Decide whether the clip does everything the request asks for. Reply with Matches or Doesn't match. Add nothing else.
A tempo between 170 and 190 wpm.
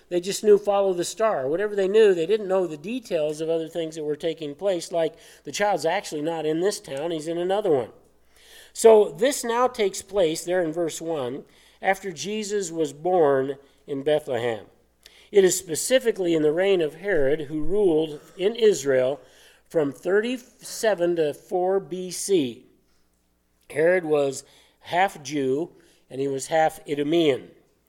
Doesn't match